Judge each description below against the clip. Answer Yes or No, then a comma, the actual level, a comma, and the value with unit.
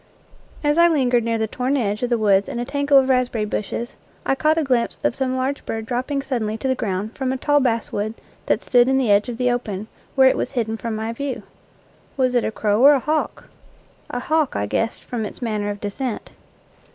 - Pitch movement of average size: Yes, average, 3.4 semitones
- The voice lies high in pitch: Yes, high, 245 Hz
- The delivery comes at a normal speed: No, fast, 225 wpm